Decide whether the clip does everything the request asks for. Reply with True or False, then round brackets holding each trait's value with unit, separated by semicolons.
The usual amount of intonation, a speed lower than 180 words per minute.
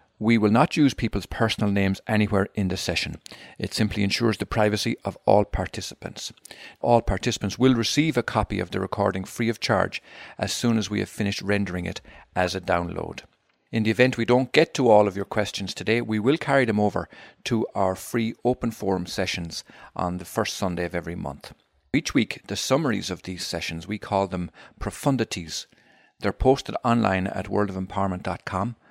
False (3.7 semitones; 185 wpm)